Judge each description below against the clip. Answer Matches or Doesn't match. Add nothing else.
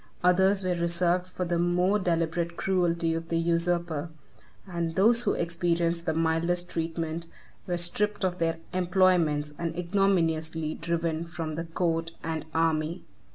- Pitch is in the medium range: Matches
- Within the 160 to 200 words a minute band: Doesn't match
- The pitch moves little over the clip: Matches